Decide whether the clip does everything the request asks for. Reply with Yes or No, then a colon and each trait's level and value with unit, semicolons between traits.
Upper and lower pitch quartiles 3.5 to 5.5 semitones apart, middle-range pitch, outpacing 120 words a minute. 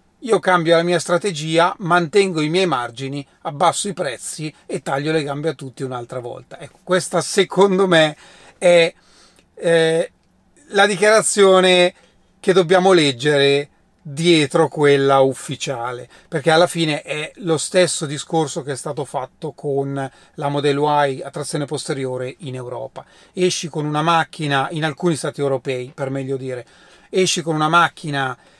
Yes: average, 4.0 semitones; medium, 160 Hz; average, 145 wpm